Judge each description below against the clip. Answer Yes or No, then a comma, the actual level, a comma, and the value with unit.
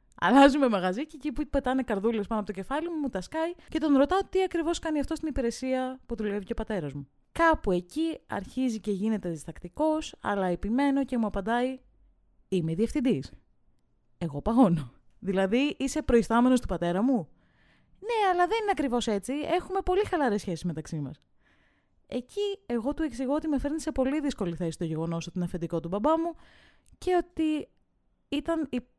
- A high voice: Yes, very high, 255 Hz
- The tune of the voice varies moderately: No, wide, 8.0 semitones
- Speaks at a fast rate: Yes, fast, 180 wpm